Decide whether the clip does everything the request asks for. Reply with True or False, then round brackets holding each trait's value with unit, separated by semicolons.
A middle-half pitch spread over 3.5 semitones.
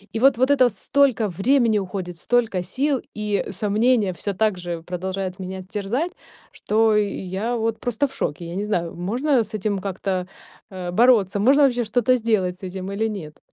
True (4.4 semitones)